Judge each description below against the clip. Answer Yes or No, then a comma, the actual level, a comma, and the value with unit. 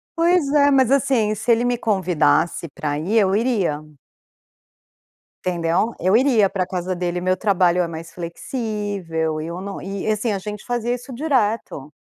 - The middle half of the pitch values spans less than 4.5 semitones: No, average, 5.2 semitones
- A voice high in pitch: Yes, high, 200 Hz